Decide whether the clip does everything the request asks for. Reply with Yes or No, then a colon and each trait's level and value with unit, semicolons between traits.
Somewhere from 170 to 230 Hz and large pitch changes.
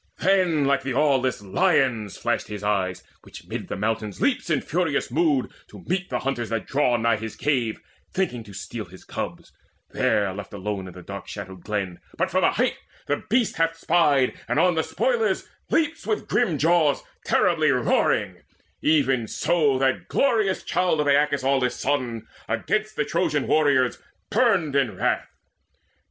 No: low, 135 Hz; wide, 6.9 semitones